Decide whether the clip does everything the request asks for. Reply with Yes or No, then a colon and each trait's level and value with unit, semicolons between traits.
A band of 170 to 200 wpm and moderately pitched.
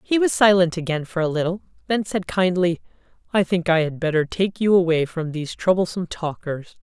Yes: average, 190 wpm; medium, 175 Hz